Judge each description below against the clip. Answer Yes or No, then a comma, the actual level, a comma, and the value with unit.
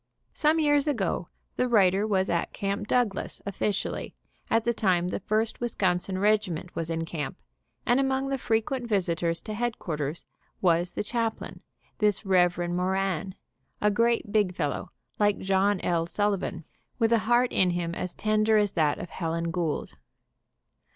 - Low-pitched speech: No, high, 195 Hz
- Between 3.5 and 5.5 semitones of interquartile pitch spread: Yes, average, 4.2 semitones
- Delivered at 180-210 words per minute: No, average, 155 wpm